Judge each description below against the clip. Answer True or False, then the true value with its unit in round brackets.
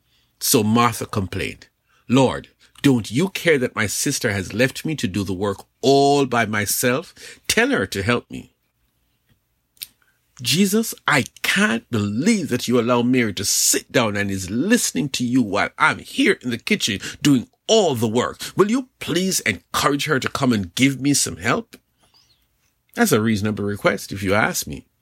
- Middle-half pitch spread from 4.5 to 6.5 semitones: True (5.1 semitones)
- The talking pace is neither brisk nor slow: True (170 wpm)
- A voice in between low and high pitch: False (125 Hz)